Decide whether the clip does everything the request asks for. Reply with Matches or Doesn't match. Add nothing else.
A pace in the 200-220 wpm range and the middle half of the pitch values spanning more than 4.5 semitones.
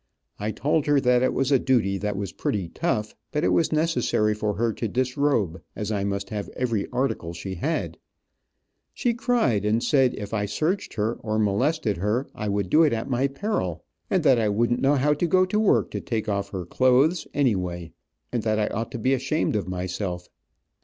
Matches